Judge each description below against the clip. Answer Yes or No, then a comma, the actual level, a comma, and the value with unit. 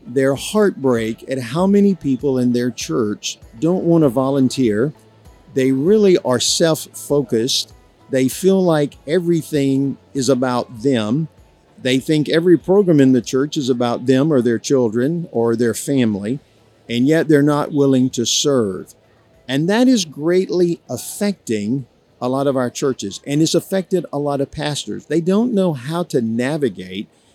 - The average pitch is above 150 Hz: No, low, 135 Hz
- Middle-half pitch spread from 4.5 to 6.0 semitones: Yes, average, 4.8 semitones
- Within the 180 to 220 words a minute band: No, average, 155 wpm